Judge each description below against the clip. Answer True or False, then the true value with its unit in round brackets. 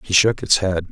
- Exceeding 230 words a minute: True (260 wpm)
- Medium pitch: False (95 Hz)